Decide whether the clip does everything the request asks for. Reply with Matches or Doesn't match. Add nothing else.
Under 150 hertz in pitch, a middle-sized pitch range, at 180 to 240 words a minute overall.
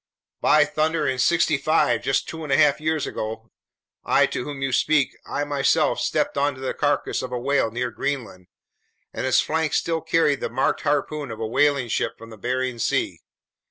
Matches